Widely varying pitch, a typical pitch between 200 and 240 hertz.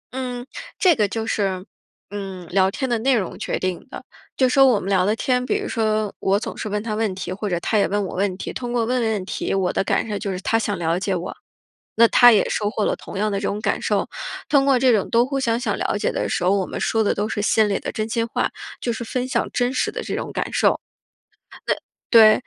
No: average, 3.5 semitones; high, 215 Hz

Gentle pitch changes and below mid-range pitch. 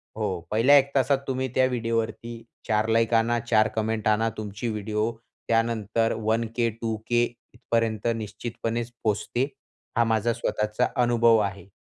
Yes: narrow, 1.5 semitones; low, 115 Hz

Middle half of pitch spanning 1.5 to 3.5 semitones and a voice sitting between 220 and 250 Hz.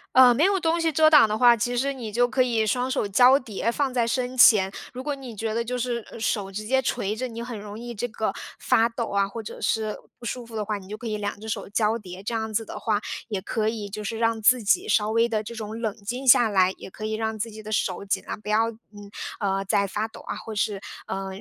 Yes: average, 2.7 semitones; high, 225 Hz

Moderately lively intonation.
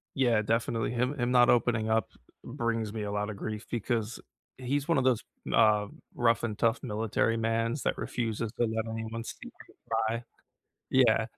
No: narrow, 1.6 semitones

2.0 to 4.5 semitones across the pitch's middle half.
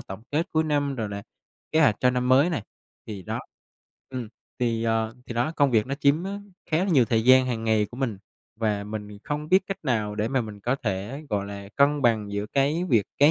No: average, 5.0 semitones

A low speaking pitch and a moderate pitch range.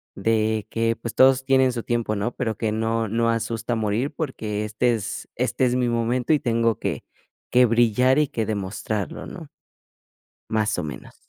No: low, 115 Hz; narrow, 2.3 semitones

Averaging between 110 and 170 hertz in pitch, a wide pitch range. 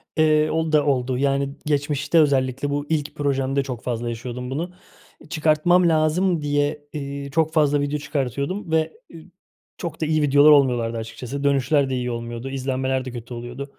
No: medium, 140 Hz; average, 2.9 semitones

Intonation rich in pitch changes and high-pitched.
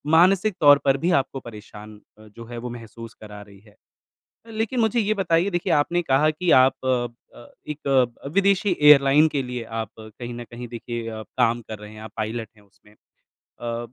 No: wide, 6.4 semitones; low, 120 Hz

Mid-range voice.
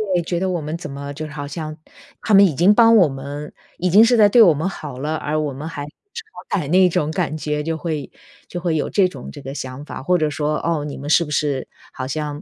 Yes: medium, 155 Hz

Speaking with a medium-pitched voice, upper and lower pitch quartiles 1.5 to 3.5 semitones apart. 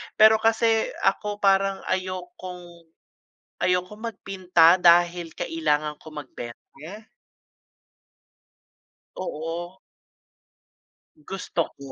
Yes: medium, 180 Hz; narrow, 2.5 semitones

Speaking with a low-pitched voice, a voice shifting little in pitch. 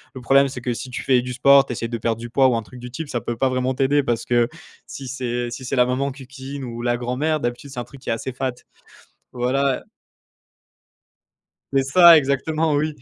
Yes: low, 130 Hz; narrow, 2.2 semitones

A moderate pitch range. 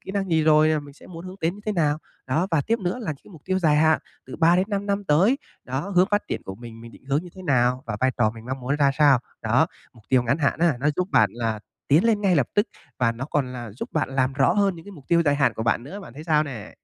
No: wide, 5.9 semitones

